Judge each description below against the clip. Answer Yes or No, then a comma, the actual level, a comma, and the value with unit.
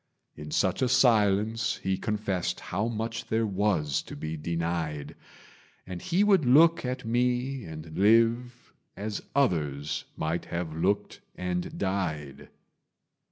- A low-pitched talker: Yes, low, 100 Hz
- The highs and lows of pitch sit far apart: Yes, wide, 5.9 semitones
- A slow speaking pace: Yes, slow, 125 wpm